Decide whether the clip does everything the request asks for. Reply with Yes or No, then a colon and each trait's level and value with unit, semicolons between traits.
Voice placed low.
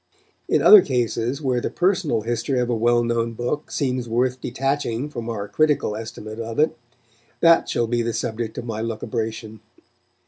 Yes: low, 120 Hz